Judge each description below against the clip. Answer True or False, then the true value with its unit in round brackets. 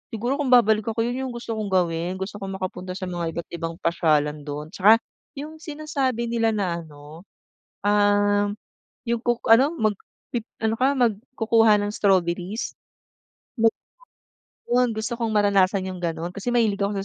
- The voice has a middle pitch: False (205 Hz)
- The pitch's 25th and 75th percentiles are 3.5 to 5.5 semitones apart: True (4.4 semitones)